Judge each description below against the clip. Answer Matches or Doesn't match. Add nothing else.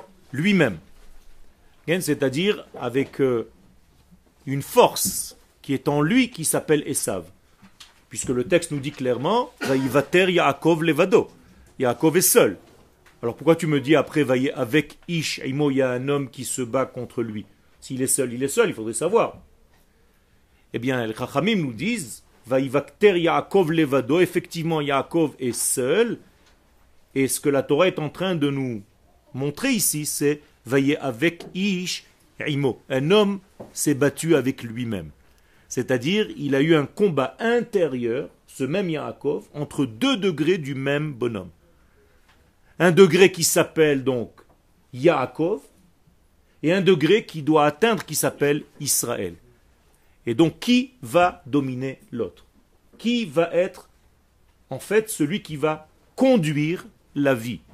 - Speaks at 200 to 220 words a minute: Doesn't match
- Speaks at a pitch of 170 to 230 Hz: Doesn't match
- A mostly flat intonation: Doesn't match